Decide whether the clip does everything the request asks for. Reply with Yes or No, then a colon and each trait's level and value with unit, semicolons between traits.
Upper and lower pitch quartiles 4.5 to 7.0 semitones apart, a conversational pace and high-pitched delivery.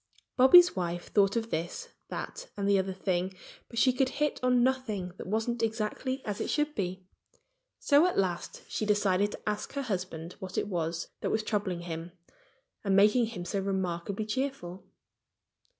Yes: average, 5.2 semitones; average, 170 wpm; high, 205 Hz